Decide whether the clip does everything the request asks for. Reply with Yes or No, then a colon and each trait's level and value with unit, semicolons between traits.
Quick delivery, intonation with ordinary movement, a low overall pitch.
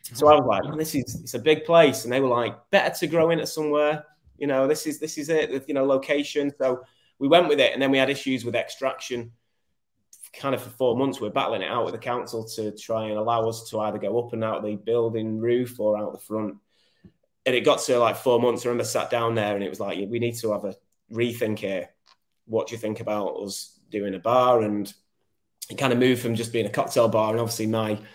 Yes: fast, 255 wpm; average, 3.9 semitones; low, 120 Hz